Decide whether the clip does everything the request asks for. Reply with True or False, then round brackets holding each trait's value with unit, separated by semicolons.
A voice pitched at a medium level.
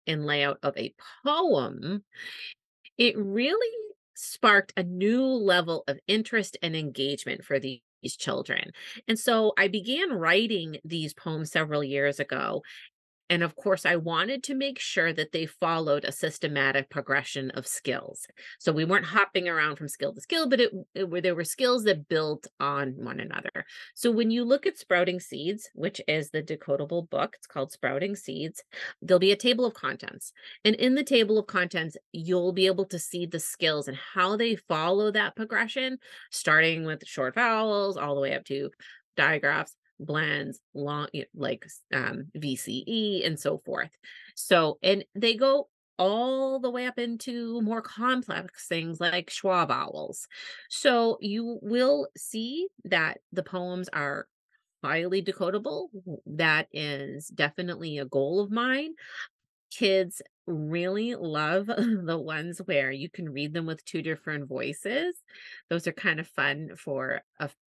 True (180 Hz)